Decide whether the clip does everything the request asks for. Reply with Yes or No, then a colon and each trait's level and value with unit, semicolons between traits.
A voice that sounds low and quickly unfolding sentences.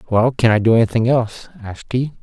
Yes: low, 115 Hz; fast, 215 wpm